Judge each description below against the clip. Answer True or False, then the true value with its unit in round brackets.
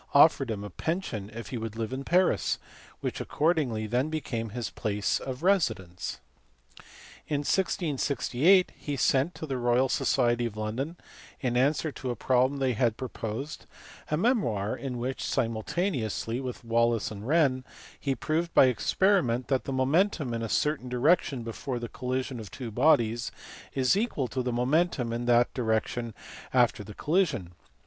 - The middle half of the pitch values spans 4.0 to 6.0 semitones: True (4.3 semitones)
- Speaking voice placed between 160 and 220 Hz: False (125 Hz)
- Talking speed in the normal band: True (160 wpm)